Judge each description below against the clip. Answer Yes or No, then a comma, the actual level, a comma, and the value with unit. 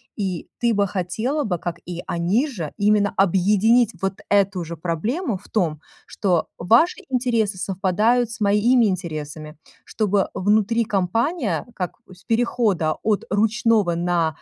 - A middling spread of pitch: Yes, average, 4.4 semitones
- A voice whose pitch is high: Yes, high, 200 Hz